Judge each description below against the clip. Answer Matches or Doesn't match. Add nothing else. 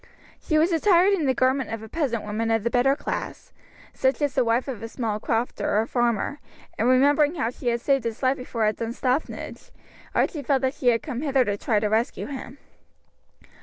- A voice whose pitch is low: Doesn't match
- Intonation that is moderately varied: Matches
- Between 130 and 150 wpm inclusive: Doesn't match